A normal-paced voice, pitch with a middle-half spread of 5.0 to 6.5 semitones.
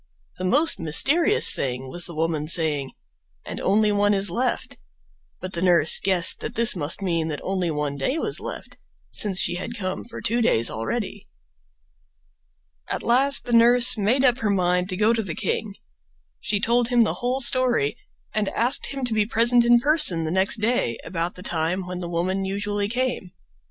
Yes: average, 185 wpm; wide, 5.5 semitones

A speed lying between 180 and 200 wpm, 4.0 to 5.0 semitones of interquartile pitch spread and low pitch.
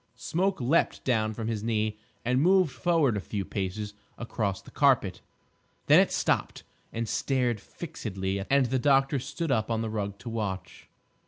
No: average, 165 wpm; average, 4.4 semitones; low, 115 Hz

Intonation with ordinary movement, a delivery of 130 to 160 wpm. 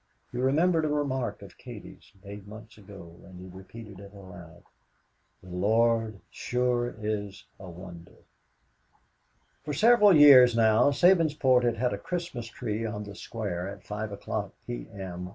Yes: average, 4.5 semitones; average, 145 wpm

